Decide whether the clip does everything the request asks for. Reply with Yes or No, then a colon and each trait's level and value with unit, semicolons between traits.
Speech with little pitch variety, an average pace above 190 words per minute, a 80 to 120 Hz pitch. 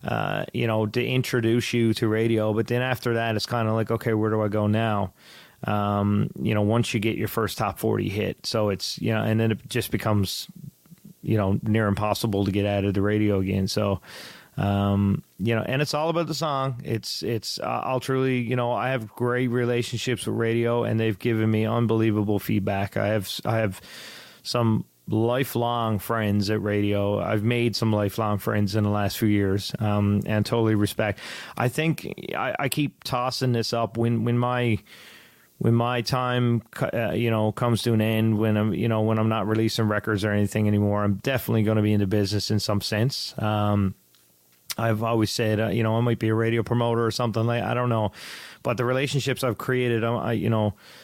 Yes: narrow, 2.3 semitones; fast, 205 wpm; low, 110 Hz